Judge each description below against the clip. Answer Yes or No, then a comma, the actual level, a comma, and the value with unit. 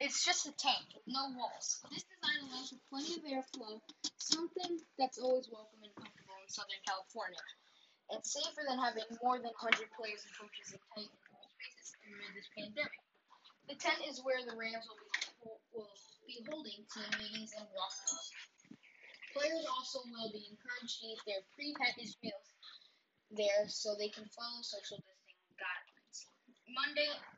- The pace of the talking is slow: No, average, 160 wpm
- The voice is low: No, high, 230 Hz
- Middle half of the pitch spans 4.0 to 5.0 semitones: Yes, average, 4.5 semitones